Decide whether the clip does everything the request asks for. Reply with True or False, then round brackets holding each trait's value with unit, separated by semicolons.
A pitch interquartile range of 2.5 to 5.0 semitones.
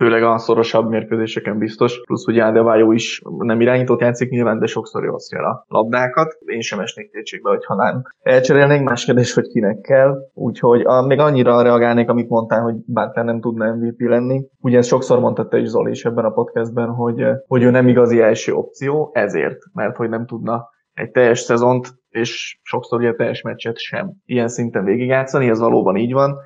False (1.9 semitones)